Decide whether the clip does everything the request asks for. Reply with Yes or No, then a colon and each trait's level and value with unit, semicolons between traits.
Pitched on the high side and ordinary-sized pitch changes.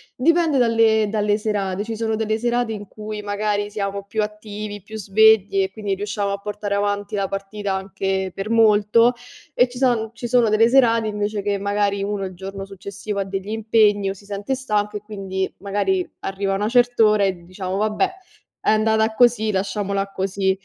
No: high, 205 Hz; narrow, 1.8 semitones